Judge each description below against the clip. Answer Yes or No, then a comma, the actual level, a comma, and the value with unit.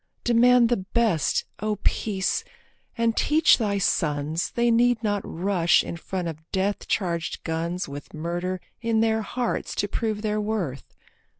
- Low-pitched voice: No, high, 205 Hz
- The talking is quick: No, average, 145 wpm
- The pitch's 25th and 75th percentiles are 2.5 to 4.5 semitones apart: No, average, 5.0 semitones